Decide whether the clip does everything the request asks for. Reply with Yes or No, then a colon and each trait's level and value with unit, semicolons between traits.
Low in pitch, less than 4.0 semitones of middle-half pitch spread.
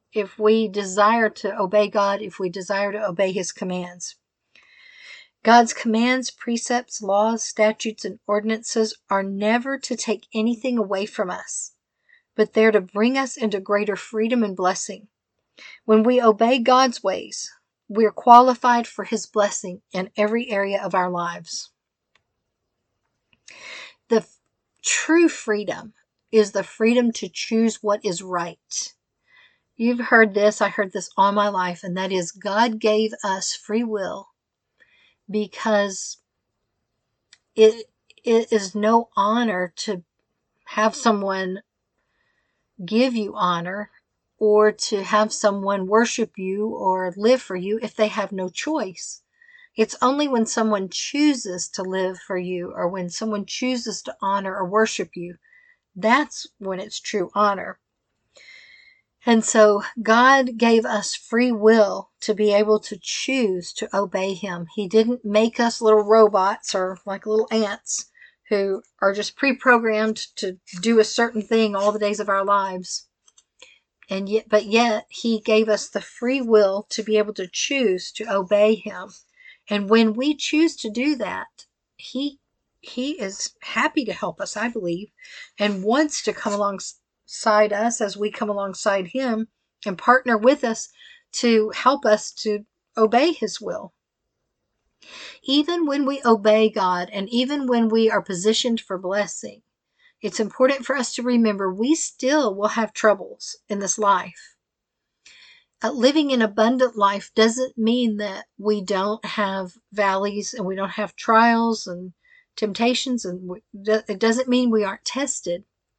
No: high, 215 Hz; average, 2.9 semitones